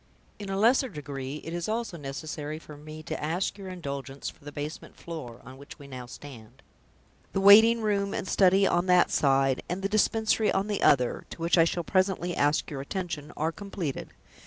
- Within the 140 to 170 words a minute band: No, average, 195 wpm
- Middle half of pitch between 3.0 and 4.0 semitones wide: No, average, 5.3 semitones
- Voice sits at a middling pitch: Yes, medium, 165 Hz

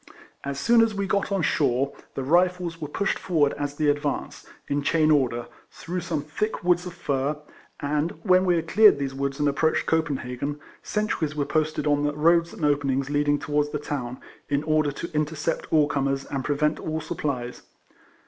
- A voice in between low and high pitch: Yes, medium, 150 Hz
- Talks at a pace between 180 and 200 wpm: Yes, average, 185 wpm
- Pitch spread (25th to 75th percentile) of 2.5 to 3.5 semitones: Yes, average, 2.9 semitones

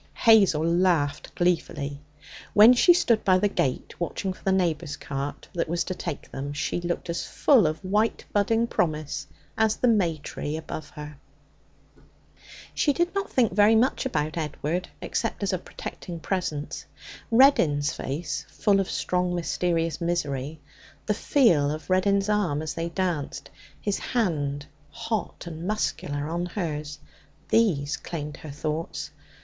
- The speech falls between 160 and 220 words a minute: No, average, 145 wpm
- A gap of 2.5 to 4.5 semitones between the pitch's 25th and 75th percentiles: No, average, 5.1 semitones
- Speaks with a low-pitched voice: No, medium, 170 Hz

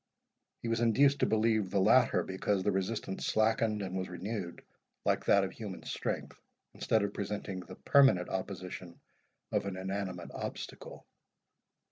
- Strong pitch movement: No, average, 2.8 semitones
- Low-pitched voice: Yes, low, 100 Hz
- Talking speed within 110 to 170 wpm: Yes, average, 145 wpm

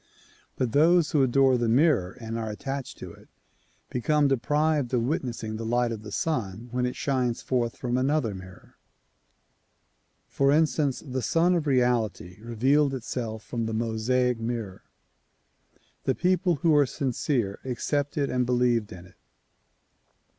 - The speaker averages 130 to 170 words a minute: Yes, average, 145 wpm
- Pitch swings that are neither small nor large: Yes, average, 3.8 semitones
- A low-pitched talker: Yes, low, 125 Hz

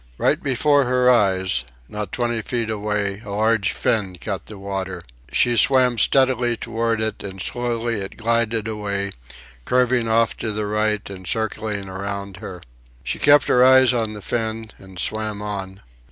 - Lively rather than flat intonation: No, average, 3.0 semitones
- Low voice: Yes, low, 110 Hz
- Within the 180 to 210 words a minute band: No, average, 160 wpm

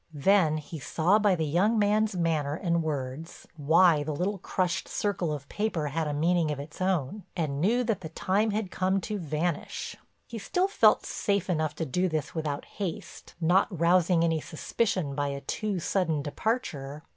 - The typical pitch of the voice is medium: Yes, medium, 170 Hz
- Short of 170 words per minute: No, average, 180 wpm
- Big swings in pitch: No, average, 4.3 semitones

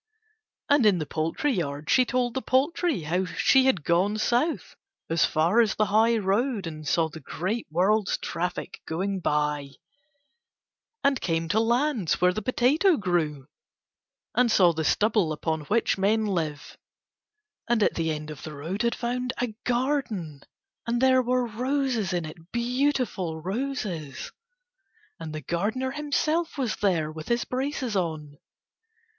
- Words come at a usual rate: Yes, average, 150 wpm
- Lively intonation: Yes, wide, 7.4 semitones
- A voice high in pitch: Yes, high, 205 Hz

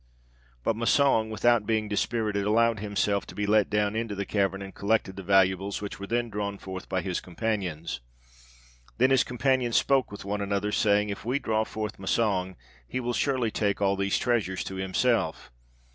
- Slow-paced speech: No, average, 180 wpm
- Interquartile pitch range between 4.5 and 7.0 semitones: No, narrow, 2.6 semitones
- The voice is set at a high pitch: No, low, 105 Hz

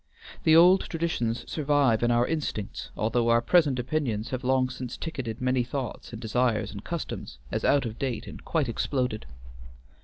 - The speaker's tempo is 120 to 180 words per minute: Yes, average, 165 wpm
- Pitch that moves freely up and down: No, average, 3.8 semitones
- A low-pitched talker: Yes, low, 125 Hz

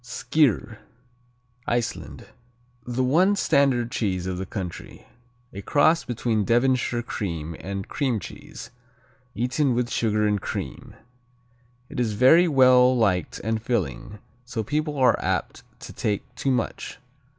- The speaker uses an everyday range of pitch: Yes, average, 3.8 semitones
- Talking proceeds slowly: Yes, slow, 130 wpm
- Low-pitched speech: Yes, low, 120 Hz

